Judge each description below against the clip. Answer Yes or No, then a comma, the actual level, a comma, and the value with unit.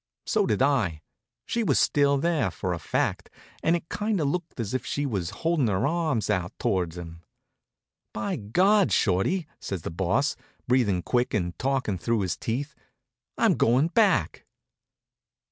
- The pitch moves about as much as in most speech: No, wide, 8.7 semitones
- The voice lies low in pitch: Yes, low, 125 Hz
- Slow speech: No, average, 160 wpm